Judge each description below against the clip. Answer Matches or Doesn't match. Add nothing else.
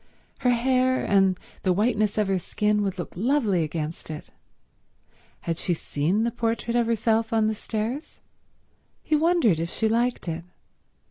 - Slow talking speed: Doesn't match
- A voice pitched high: Matches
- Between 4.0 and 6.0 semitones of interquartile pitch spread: Matches